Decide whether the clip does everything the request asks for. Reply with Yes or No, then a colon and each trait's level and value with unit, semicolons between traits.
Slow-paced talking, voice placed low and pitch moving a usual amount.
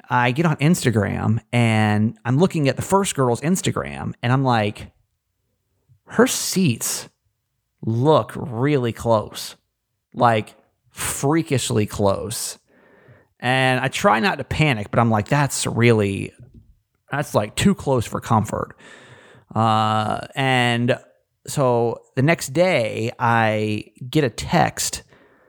Yes: slow, 120 wpm; low, 120 Hz; average, 4.0 semitones